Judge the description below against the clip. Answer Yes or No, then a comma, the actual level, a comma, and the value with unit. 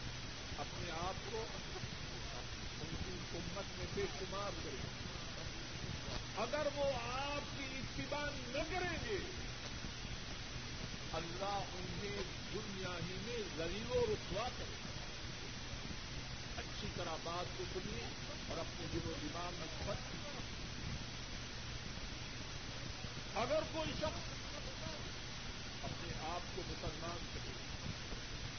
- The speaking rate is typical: No, slow, 95 wpm